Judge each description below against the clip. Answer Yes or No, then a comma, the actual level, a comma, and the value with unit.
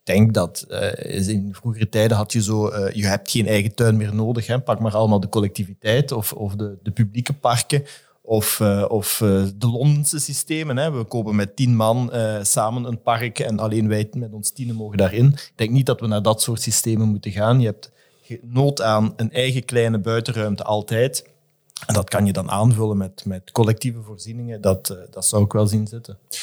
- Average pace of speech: No, fast, 210 wpm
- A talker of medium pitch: No, low, 110 Hz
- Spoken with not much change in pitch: Yes, narrow, 2.3 semitones